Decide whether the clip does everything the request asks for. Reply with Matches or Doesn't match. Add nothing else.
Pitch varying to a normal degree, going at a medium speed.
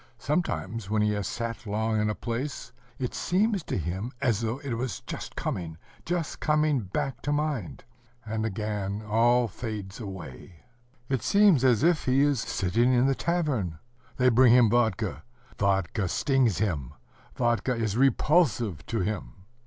Matches